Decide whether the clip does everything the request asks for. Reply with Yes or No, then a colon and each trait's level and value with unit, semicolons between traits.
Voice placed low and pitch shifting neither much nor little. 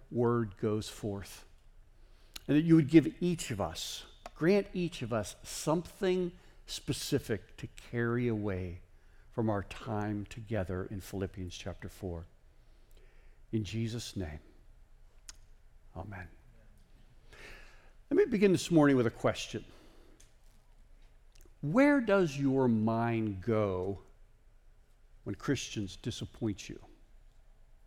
No: low, 110 Hz; wide, 6.1 semitones